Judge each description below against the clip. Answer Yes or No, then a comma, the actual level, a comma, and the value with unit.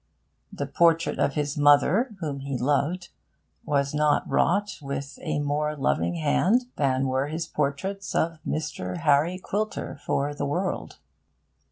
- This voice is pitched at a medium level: Yes, medium, 150 Hz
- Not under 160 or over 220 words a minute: No, average, 140 wpm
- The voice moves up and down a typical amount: Yes, average, 3.4 semitones